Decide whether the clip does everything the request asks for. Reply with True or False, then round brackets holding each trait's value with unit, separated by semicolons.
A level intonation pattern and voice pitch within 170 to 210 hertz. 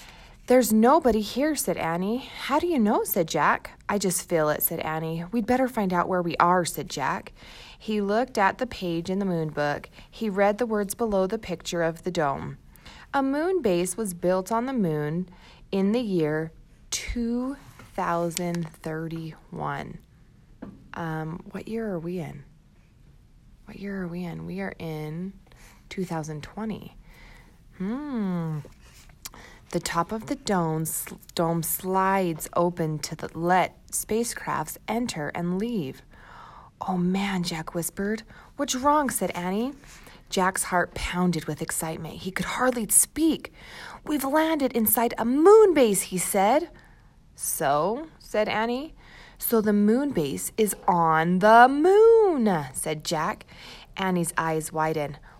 False (5.3 semitones; 190 Hz)